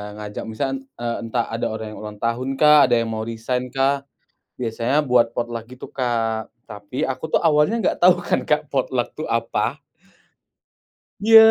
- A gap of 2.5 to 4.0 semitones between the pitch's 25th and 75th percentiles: Yes, average, 3.4 semitones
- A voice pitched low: Yes, low, 120 Hz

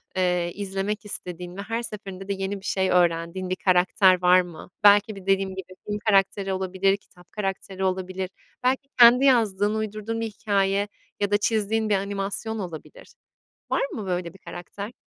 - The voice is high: Yes, high, 195 Hz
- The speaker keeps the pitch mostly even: Yes, narrow, 2.1 semitones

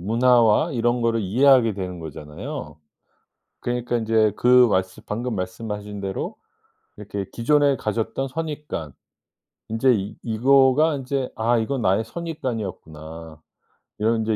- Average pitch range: Yes, average, 4.5 semitones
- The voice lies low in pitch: Yes, low, 115 Hz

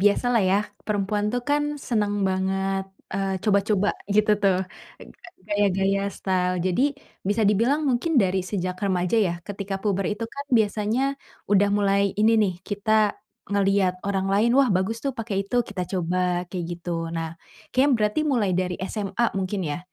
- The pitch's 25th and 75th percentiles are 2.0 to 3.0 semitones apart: Yes, narrow, 2.4 semitones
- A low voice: No, high, 200 Hz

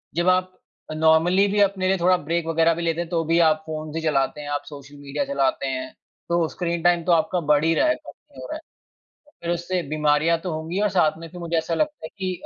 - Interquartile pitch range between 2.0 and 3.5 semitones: Yes, narrow, 2.6 semitones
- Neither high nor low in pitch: Yes, medium, 165 Hz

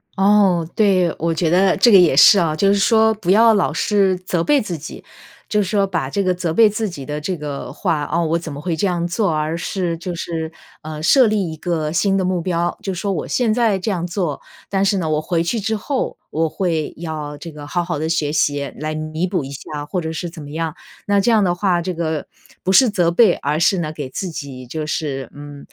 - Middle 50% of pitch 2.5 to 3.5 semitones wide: No, average, 3.9 semitones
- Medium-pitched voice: Yes, medium, 170 Hz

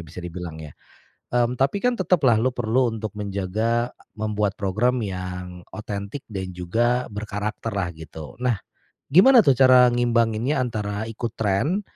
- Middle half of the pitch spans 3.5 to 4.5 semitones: Yes, average, 4.1 semitones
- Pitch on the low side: Yes, low, 110 Hz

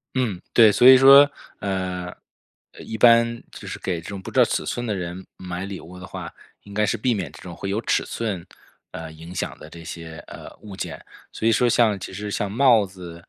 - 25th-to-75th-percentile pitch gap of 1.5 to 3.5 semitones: No, average, 4.3 semitones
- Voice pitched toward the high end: No, low, 100 Hz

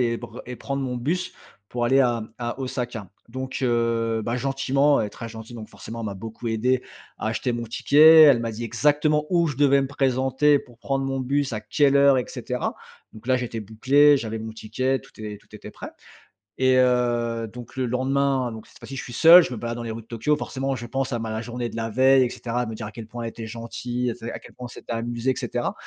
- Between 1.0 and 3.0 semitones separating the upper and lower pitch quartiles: Yes, average, 2.7 semitones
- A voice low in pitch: Yes, low, 125 Hz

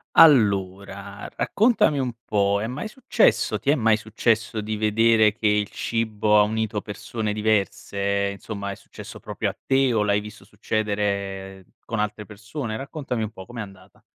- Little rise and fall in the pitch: Yes, narrow, 2.1 semitones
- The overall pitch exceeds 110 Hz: No, low, 105 Hz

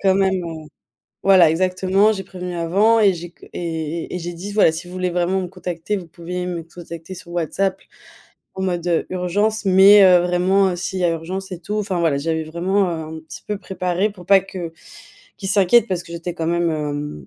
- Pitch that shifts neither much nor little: No, narrow, 2.3 semitones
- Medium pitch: Yes, medium, 180 Hz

